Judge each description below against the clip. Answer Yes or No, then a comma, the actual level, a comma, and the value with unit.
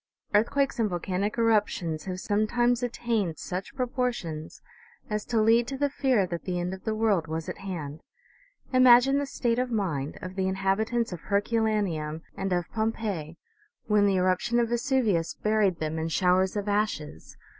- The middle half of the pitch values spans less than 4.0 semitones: No, average, 4.6 semitones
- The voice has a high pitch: Yes, high, 205 Hz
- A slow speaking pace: No, average, 165 wpm